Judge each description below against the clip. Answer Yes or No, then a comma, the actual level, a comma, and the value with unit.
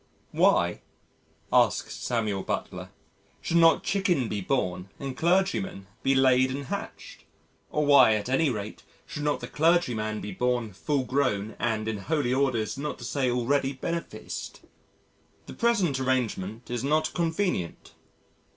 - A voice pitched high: No, low, 130 Hz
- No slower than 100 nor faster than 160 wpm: Yes, average, 140 wpm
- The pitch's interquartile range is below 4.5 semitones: No, average, 5.3 semitones